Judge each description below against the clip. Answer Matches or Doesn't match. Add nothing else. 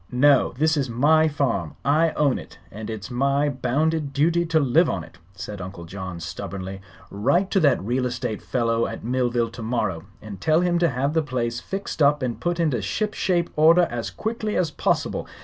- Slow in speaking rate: Doesn't match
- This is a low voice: Matches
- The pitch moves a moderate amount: Doesn't match